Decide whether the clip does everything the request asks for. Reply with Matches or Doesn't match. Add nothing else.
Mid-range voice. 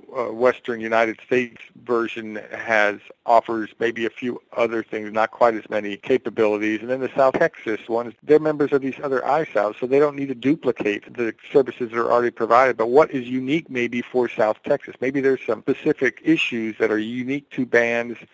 Doesn't match